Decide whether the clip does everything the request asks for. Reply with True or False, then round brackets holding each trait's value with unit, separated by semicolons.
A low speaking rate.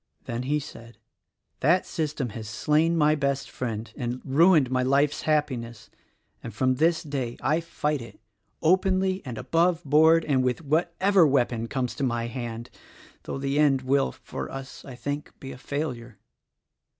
False (155 wpm)